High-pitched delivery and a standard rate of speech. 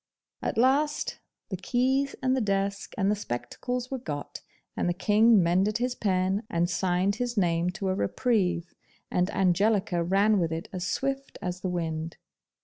Yes: high, 195 Hz; average, 165 wpm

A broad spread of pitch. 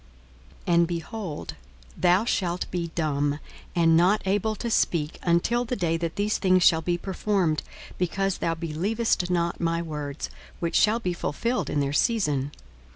No: average, 3.4 semitones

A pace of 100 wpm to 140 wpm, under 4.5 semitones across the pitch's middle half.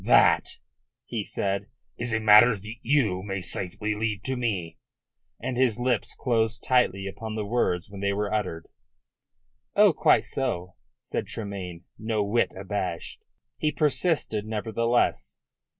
Yes: slow, 135 wpm; average, 3.3 semitones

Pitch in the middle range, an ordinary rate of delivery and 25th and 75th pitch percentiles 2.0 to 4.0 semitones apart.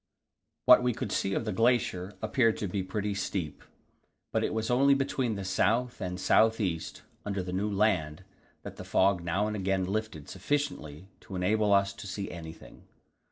No: low, 100 Hz; average, 180 wpm; average, 3.2 semitones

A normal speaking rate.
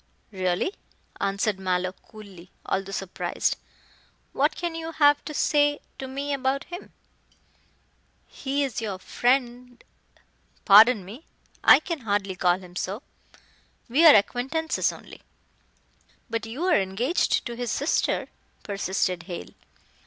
No: slow, 125 wpm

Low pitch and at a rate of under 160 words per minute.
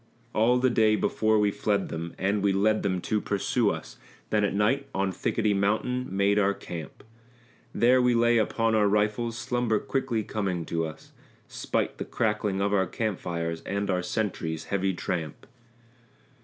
No: low, 105 Hz; average, 170 wpm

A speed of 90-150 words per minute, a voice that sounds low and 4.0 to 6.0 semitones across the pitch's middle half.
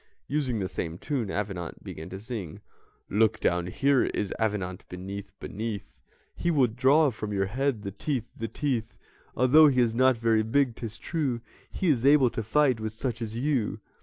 No: average, 180 wpm; low, 115 Hz; average, 4.5 semitones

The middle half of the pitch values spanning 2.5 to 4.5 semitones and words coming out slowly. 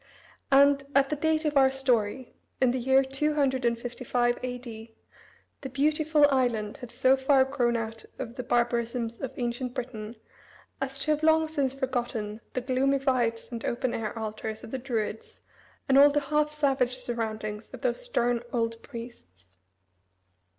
No: average, 2.8 semitones; average, 155 wpm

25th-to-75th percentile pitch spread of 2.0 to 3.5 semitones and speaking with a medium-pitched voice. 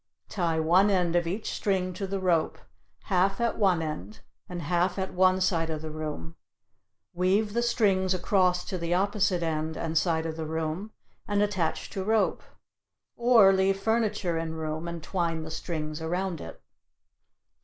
Yes: average, 3.2 semitones; medium, 180 Hz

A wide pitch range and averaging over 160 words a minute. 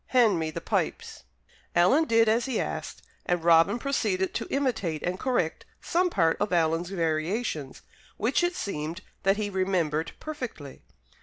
No: wide, 6.5 semitones; average, 150 wpm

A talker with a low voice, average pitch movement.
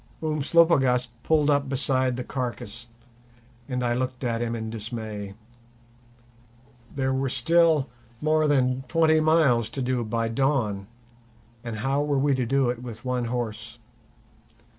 Yes: low, 125 Hz; average, 3.2 semitones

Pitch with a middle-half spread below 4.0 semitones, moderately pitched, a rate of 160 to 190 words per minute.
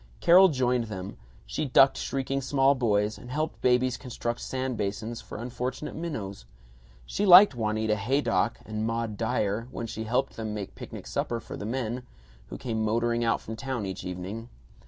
No: average, 3.3 semitones; low, 115 Hz; average, 170 wpm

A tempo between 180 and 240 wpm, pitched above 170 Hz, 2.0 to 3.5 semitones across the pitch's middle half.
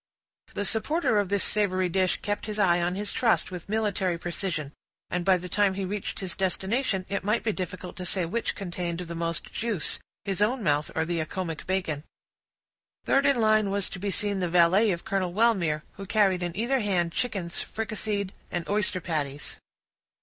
Yes: average, 190 wpm; high, 190 Hz; average, 3.2 semitones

